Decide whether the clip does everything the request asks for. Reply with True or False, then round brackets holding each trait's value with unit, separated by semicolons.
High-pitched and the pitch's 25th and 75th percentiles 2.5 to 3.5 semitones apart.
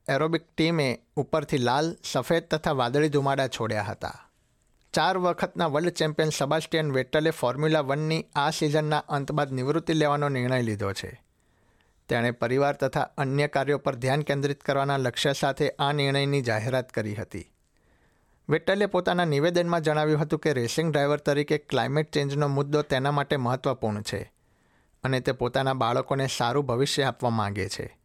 False (140 Hz; 3.1 semitones)